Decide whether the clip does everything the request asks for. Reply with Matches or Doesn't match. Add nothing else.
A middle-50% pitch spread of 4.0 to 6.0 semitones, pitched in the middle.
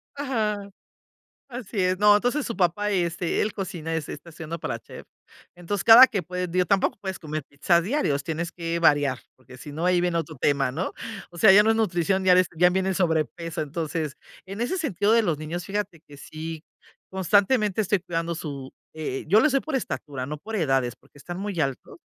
Matches